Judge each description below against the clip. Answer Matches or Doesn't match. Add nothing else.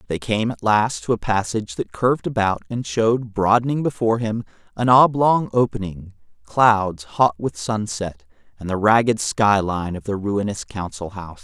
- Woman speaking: Doesn't match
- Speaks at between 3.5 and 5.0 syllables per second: Matches